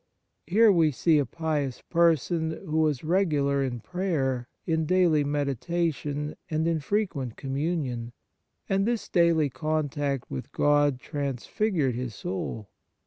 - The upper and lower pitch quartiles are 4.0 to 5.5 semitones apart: No, average, 3.6 semitones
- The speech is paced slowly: Yes, slow, 125 wpm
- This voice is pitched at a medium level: Yes, medium, 155 Hz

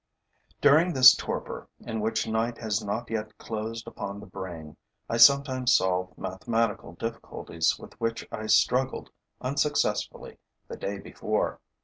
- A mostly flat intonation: No, average, 3.3 semitones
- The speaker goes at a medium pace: No, slow, 130 wpm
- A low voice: Yes, low, 110 Hz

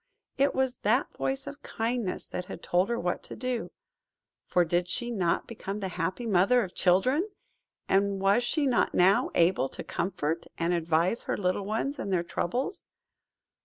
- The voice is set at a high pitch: Yes, high, 195 Hz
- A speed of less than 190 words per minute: Yes, average, 170 wpm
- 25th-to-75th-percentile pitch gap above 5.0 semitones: Yes, wide, 5.5 semitones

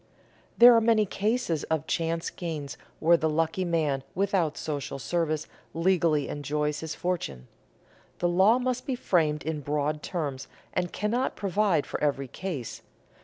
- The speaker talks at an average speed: Yes, average, 145 wpm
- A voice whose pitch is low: No, medium, 165 Hz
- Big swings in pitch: No, average, 4.2 semitones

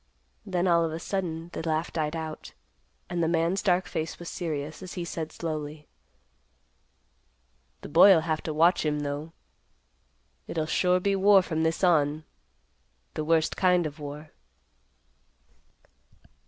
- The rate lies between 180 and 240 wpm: No, average, 140 wpm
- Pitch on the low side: No, medium, 165 Hz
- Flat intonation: Yes, narrow, 2.3 semitones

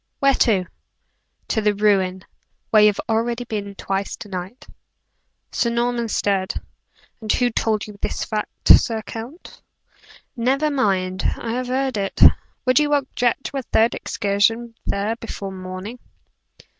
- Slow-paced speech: No, average, 145 wpm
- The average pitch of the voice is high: Yes, high, 225 Hz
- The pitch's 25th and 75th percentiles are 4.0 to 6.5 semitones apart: No, average, 3.5 semitones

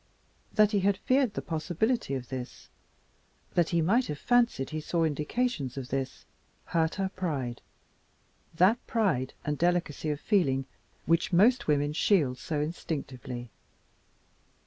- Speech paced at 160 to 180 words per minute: No, slow, 135 wpm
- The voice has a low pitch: No, medium, 160 Hz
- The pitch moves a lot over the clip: Yes, wide, 6.3 semitones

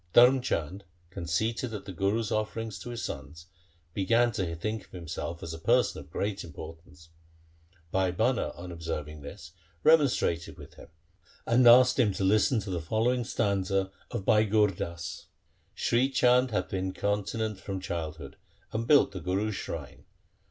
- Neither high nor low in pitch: No, low, 100 Hz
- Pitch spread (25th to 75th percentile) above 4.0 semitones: Yes, average, 5.1 semitones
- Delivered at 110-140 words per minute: No, average, 160 wpm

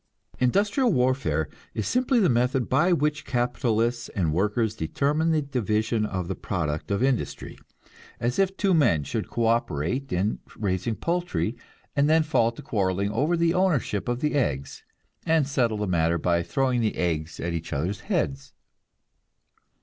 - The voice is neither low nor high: No, low, 120 Hz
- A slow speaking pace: No, average, 155 wpm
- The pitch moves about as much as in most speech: No, wide, 8.0 semitones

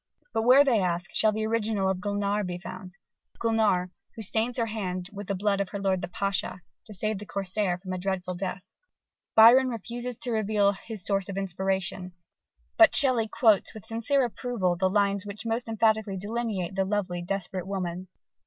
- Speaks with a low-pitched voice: No, high, 200 Hz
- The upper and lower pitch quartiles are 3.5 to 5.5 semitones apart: No, average, 2.9 semitones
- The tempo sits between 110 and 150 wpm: No, average, 185 wpm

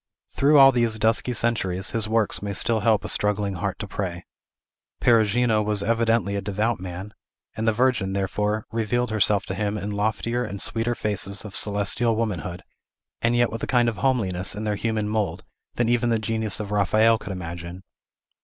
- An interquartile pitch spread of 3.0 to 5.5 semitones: No, narrow, 2.4 semitones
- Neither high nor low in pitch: No, low, 105 Hz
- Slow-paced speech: No, average, 180 wpm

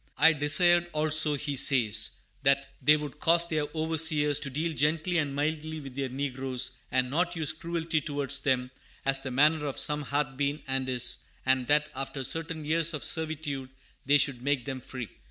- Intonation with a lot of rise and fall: No, average, 2.8 semitones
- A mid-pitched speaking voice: Yes, medium, 145 Hz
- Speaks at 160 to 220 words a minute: Yes, average, 180 wpm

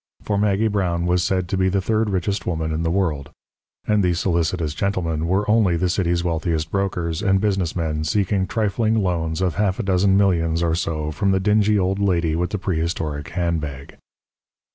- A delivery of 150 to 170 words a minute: No, average, 185 wpm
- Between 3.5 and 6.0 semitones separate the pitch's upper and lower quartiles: No, average, 3.1 semitones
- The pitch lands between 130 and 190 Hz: No, very low, 90 Hz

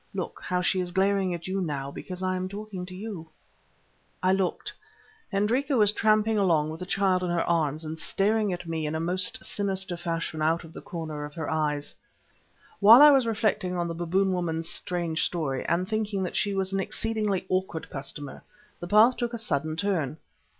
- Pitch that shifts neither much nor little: Yes, average, 3.6 semitones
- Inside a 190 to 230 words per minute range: Yes, average, 195 wpm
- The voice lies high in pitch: No, medium, 180 Hz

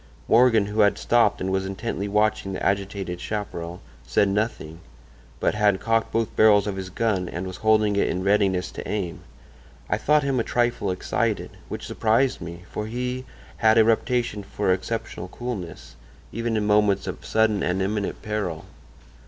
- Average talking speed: Yes, average, 170 wpm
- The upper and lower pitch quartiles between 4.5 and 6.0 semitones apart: No, average, 2.9 semitones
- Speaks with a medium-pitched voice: No, low, 105 Hz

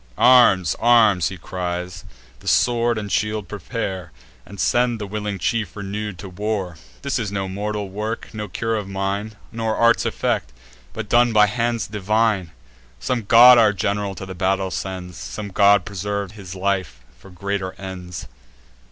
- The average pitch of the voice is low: Yes, low, 100 Hz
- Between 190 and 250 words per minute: No, average, 160 wpm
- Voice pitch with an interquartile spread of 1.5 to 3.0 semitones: Yes, average, 2.7 semitones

